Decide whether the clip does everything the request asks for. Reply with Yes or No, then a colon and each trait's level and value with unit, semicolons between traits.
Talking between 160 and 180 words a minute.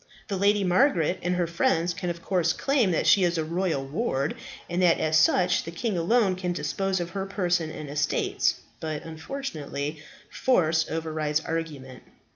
Yes: average, 170 wpm